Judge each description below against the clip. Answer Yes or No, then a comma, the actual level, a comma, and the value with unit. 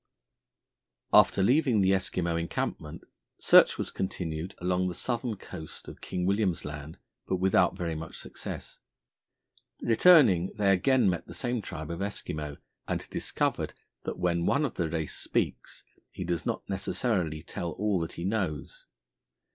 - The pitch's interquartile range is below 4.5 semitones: Yes, average, 4.1 semitones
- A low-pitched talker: Yes, very low, 90 Hz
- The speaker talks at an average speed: Yes, average, 145 wpm